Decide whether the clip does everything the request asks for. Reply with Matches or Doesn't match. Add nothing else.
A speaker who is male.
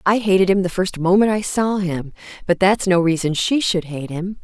Doesn't match